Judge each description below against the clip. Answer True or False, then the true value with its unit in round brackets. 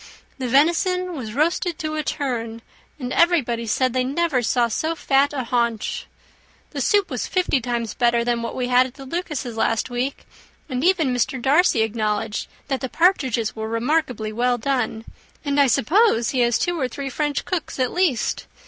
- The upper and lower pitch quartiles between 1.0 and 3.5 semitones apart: False (4.6 semitones)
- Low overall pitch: False (255 Hz)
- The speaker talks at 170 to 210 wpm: True (180 wpm)